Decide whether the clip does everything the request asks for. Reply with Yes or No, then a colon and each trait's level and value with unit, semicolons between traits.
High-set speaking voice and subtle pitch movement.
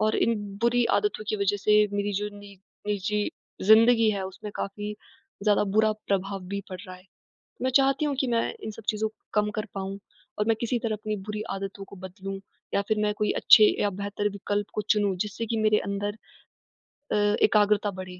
Yes: high, 210 Hz; narrow, 1.4 semitones